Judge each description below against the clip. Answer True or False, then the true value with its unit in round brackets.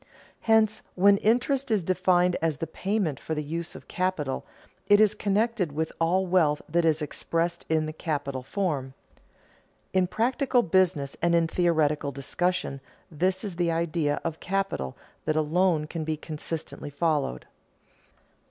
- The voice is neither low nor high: True (170 Hz)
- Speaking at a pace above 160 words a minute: False (145 wpm)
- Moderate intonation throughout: True (3.6 semitones)